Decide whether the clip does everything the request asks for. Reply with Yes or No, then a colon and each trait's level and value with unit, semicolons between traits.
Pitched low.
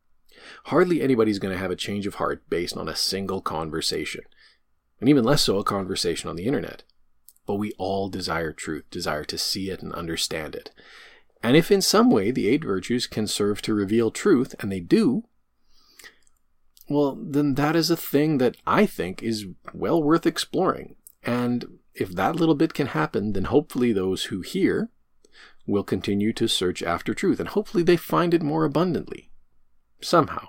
Yes: low, 115 Hz